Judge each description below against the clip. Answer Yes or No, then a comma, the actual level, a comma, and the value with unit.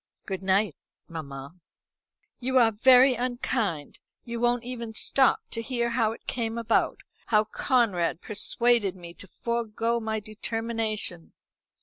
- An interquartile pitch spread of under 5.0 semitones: Yes, average, 3.2 semitones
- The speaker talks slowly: Yes, slow, 125 wpm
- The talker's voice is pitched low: No, high, 225 Hz